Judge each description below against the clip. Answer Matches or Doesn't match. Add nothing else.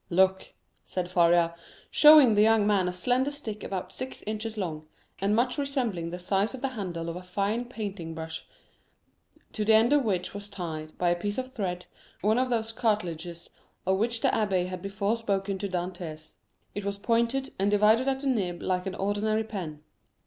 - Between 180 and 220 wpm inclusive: Matches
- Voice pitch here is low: Doesn't match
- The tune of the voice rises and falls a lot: Doesn't match